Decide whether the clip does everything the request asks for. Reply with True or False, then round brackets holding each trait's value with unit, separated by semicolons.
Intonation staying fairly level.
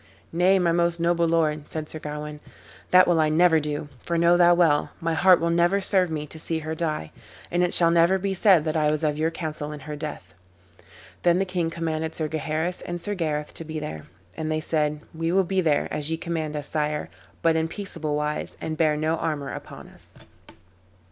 True (2.1 semitones)